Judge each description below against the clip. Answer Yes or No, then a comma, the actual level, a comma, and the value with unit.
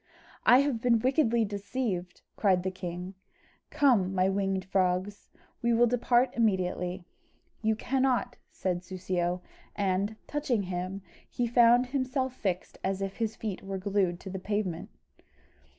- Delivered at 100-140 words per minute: Yes, slow, 135 wpm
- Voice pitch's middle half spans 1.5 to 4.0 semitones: No, average, 4.5 semitones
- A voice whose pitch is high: Yes, high, 200 Hz